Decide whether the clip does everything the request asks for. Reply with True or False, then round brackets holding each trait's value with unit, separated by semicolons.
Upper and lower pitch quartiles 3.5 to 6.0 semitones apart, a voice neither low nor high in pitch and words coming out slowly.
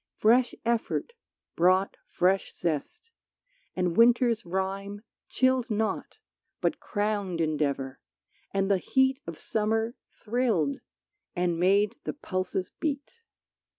False (4.7 semitones; 205 Hz; 105 wpm)